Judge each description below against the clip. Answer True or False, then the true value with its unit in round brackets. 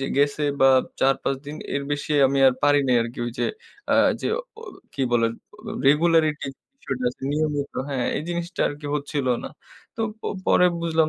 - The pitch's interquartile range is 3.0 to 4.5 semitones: False (2.4 semitones)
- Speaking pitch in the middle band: True (145 Hz)